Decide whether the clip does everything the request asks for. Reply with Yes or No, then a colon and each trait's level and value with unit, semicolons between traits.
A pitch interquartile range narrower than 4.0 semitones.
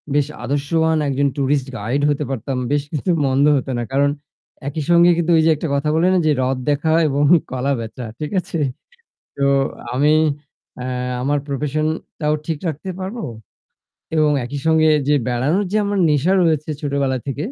Yes: average, 2.8 semitones